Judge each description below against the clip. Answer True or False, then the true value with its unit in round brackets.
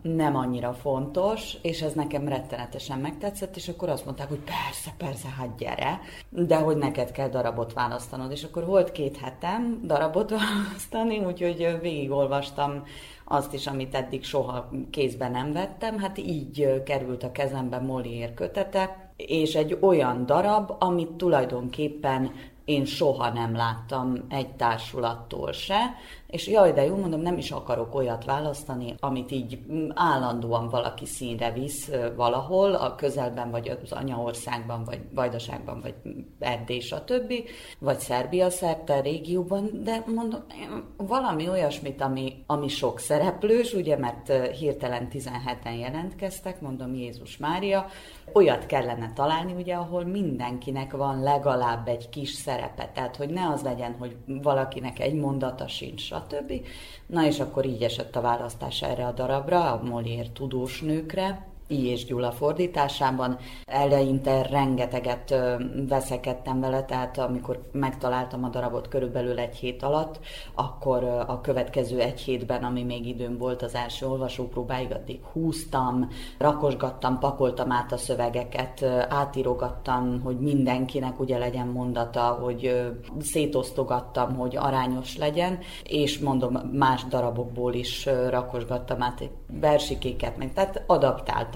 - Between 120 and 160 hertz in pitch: True (135 Hz)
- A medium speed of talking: True (135 wpm)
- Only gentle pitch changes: False (3.3 semitones)